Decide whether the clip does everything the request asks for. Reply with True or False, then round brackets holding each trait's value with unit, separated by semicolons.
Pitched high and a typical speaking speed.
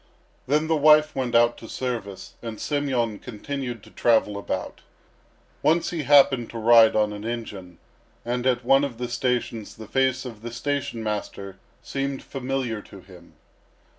False (120 Hz; 160 wpm)